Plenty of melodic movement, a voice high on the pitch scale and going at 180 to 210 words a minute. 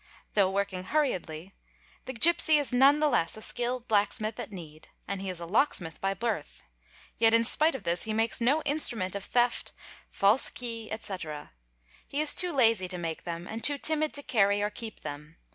Yes: wide, 5.7 semitones; high, 215 Hz; average, 195 wpm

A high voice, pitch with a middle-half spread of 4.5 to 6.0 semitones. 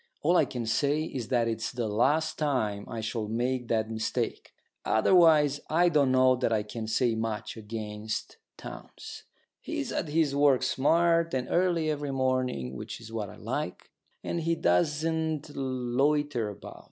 No: low, 130 Hz; average, 5.2 semitones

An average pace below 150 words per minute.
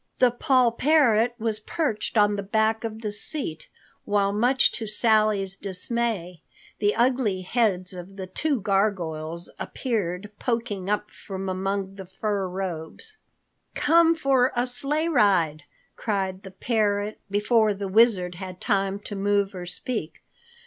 Yes: average, 140 wpm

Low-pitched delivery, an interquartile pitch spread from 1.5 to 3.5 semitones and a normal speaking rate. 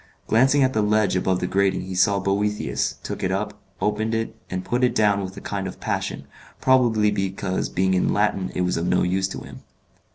No: low, 100 Hz; narrow, 2.5 semitones; fast, 215 wpm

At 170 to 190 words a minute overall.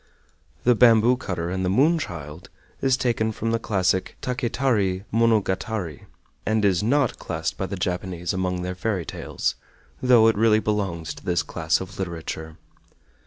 No: average, 155 wpm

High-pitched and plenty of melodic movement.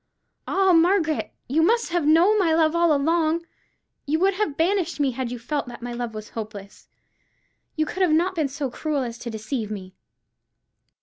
Yes: very high, 310 Hz; wide, 5.9 semitones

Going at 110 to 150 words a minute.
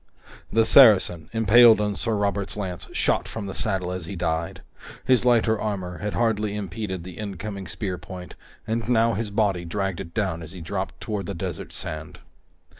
No: average, 180 wpm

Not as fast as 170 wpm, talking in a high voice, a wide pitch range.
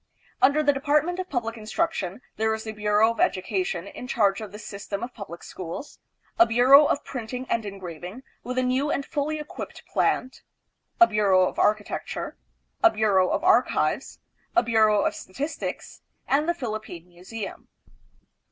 Yes: average, 160 wpm; high, 225 Hz; wide, 5.7 semitones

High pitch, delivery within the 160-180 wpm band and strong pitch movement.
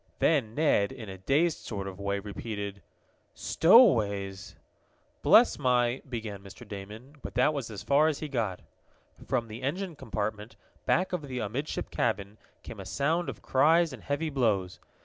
No: low, 120 Hz; average, 165 wpm; wide, 6.3 semitones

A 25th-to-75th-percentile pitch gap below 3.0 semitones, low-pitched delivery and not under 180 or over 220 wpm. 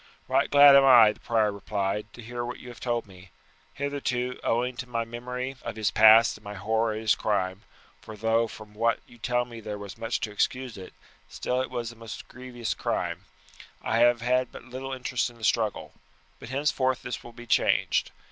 Yes: narrow, 2.6 semitones; low, 115 Hz; fast, 205 wpm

